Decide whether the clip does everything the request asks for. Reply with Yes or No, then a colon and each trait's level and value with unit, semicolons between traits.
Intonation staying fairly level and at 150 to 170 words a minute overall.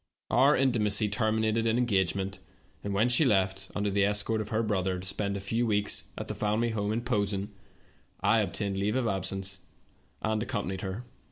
No: narrow, 2.2 semitones; average, 185 wpm